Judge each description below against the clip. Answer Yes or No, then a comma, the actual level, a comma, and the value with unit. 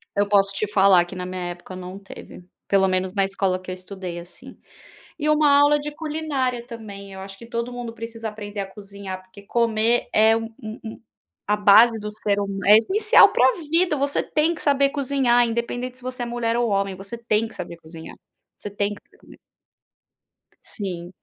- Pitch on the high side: Yes, high, 215 Hz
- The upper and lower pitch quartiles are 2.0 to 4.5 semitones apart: Yes, average, 3.8 semitones